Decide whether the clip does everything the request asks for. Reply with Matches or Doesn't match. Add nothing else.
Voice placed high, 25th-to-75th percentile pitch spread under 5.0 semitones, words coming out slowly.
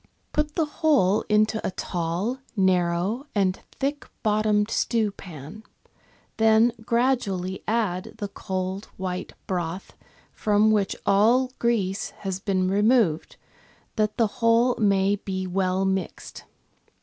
Matches